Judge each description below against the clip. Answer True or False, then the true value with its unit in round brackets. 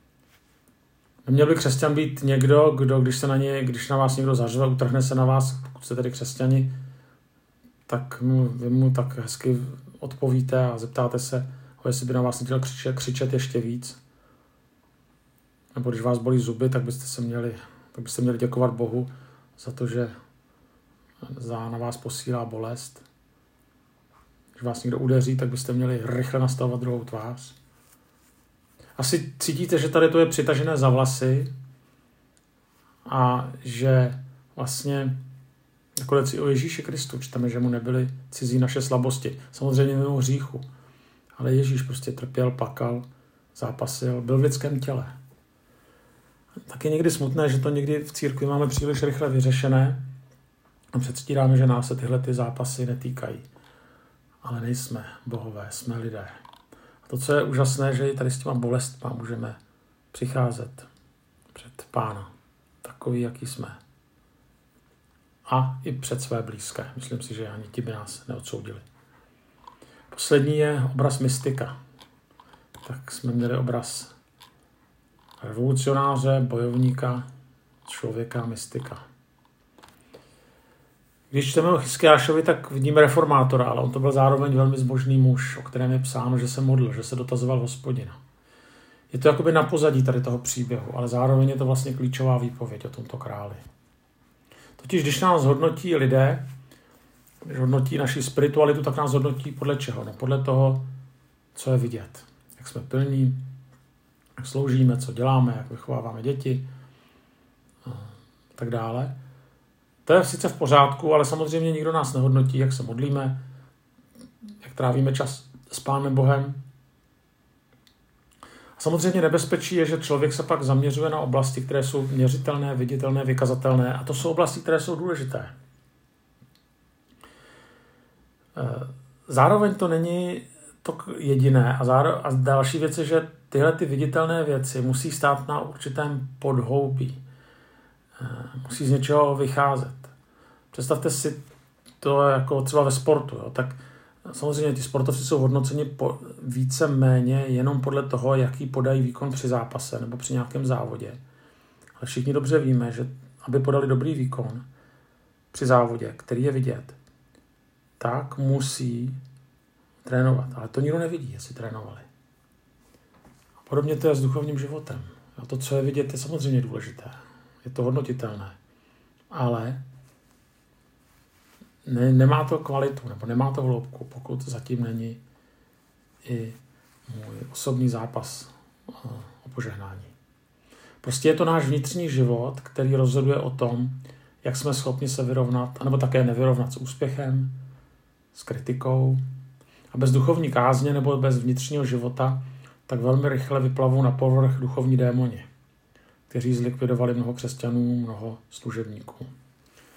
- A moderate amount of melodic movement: False (1.7 semitones)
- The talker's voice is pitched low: True (130 Hz)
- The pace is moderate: True (135 wpm)